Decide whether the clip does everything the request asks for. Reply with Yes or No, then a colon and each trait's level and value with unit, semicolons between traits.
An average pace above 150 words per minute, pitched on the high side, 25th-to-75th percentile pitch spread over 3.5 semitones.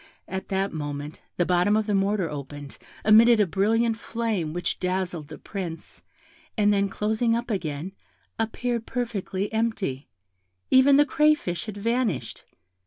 No: average, 140 wpm; high, 200 Hz; average, 4.6 semitones